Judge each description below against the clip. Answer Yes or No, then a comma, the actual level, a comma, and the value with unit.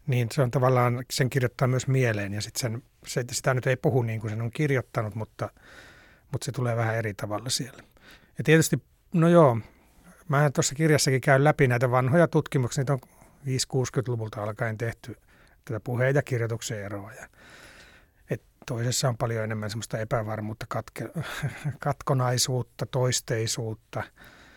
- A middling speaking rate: Yes, average, 145 wpm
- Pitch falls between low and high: No, low, 125 Hz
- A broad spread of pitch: No, average, 3.4 semitones